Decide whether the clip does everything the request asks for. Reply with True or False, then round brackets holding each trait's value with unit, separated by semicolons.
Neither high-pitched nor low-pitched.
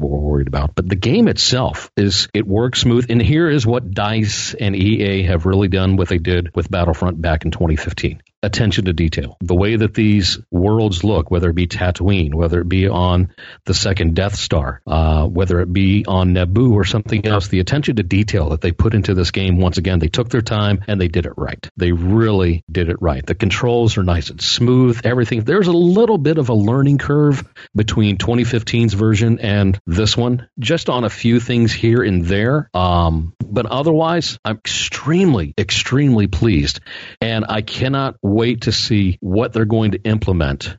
False (100 Hz)